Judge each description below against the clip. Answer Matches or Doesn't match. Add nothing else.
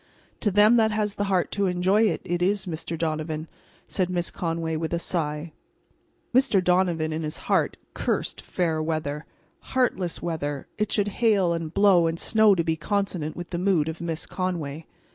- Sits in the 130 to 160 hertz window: Doesn't match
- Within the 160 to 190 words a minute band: Matches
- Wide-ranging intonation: Doesn't match